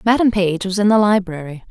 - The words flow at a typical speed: No, fast, 210 wpm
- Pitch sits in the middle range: No, high, 195 Hz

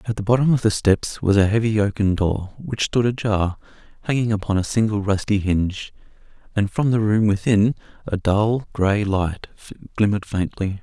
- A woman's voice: No, male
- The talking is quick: No, average, 170 wpm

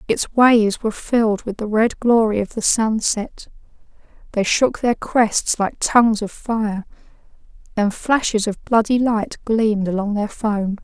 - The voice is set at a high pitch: Yes, high, 220 Hz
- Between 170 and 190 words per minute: No, average, 155 wpm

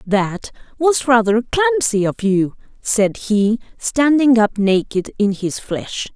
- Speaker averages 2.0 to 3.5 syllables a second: Yes, 3.4 syllables/s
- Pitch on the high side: Yes, high, 225 Hz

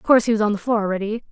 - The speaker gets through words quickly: Yes, fast, 365 wpm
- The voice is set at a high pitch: Yes, high, 215 Hz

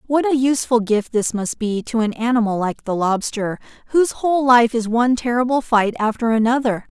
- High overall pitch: Yes, high, 235 Hz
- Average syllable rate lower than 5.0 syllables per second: No, 5.5 syllables/s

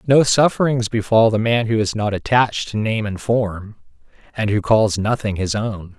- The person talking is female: No, male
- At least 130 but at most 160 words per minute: No, average, 190 wpm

